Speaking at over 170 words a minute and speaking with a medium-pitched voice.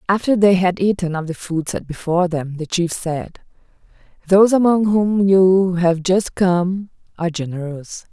No: average, 165 wpm; medium, 180 Hz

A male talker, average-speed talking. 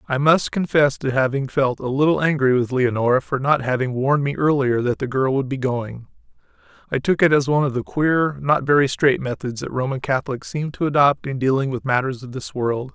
No: male; fast, 220 wpm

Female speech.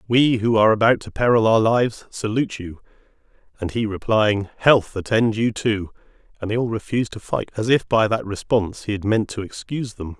No: male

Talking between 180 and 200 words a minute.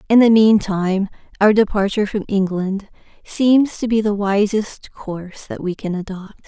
No: average, 155 wpm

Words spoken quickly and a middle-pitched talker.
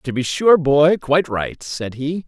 Yes: fast, 210 wpm; medium, 150 Hz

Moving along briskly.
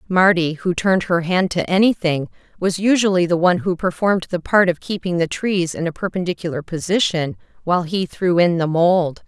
No: average, 190 wpm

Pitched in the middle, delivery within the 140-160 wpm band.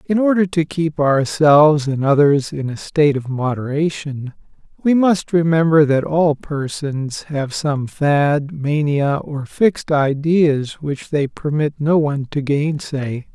Yes: medium, 150 Hz; average, 145 wpm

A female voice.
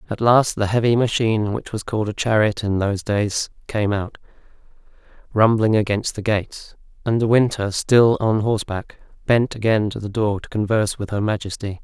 No: male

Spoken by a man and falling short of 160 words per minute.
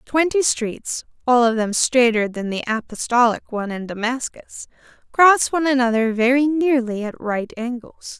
No: female; average, 145 wpm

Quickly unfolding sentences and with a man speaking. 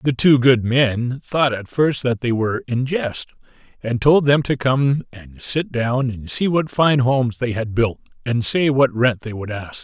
Yes: fast, 215 wpm; male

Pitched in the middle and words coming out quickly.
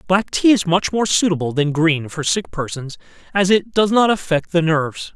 Yes: medium, 175 Hz; fast, 210 wpm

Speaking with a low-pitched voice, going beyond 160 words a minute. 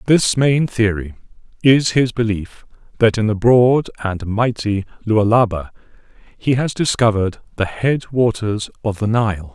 No: low, 110 Hz; average, 140 wpm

